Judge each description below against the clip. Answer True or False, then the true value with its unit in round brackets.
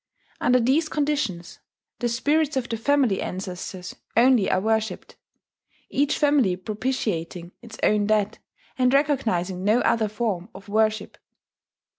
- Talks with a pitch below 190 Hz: False (220 Hz)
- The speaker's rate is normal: False (125 wpm)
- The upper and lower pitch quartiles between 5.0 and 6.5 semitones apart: True (5.3 semitones)